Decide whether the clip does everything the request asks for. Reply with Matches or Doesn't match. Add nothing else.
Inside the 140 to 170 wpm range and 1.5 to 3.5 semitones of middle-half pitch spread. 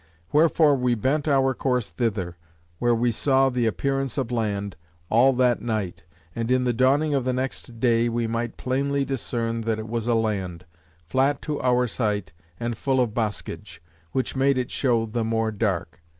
Doesn't match